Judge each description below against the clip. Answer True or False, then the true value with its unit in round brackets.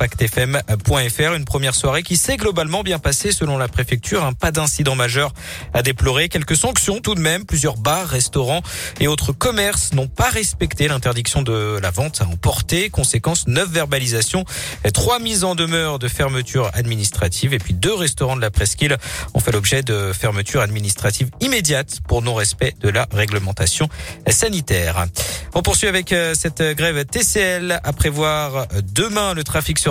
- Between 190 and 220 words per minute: False (160 wpm)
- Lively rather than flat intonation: True (6.2 semitones)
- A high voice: False (135 Hz)